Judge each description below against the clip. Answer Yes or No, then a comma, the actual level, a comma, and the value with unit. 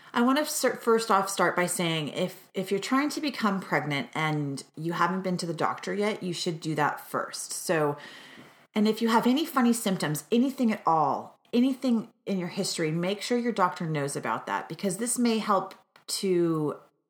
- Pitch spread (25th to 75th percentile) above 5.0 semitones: Yes, wide, 5.5 semitones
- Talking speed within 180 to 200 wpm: Yes, average, 195 wpm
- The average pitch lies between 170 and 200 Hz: Yes, high, 190 Hz